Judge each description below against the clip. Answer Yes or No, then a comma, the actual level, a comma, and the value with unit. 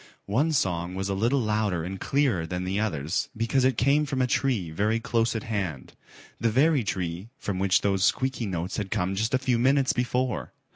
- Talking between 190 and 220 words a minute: Yes, average, 200 wpm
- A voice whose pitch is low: Yes, low, 110 Hz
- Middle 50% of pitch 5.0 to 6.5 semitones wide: Yes, average, 5.3 semitones